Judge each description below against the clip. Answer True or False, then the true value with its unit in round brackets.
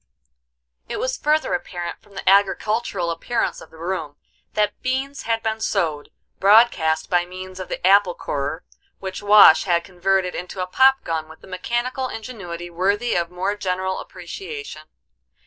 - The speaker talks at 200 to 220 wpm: False (155 wpm)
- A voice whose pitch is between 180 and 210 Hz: True (190 Hz)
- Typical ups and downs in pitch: True (4.4 semitones)